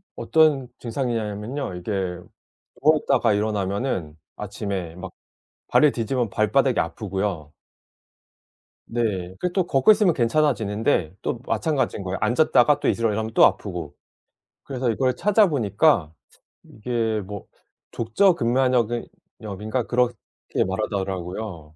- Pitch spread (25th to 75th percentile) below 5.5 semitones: Yes, average, 5.1 semitones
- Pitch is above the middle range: No, low, 110 Hz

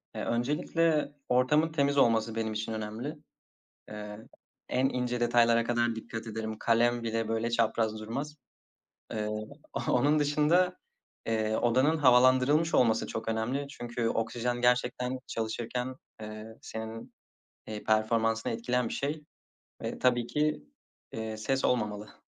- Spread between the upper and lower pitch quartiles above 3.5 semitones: No, average, 2.7 semitones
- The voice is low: Yes, low, 120 Hz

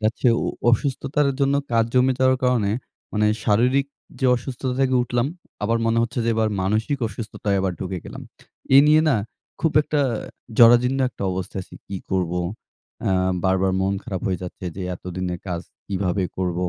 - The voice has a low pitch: Yes, low, 110 Hz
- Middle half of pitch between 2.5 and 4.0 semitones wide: No, average, 5.3 semitones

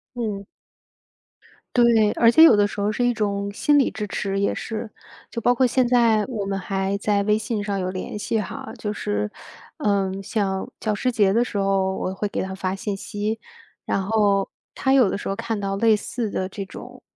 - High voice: Yes, high, 210 Hz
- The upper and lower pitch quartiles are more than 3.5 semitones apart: No, average, 2.7 semitones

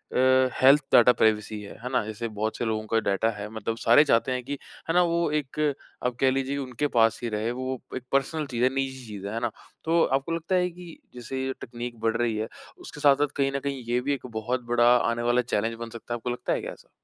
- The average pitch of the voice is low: Yes, low, 125 Hz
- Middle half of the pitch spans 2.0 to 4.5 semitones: Yes, average, 3.1 semitones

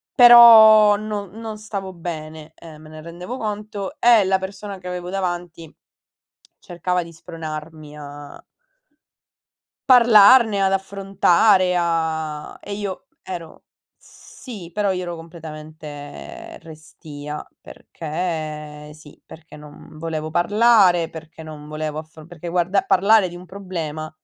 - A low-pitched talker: No, medium, 175 Hz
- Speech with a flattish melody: No, average, 4.1 semitones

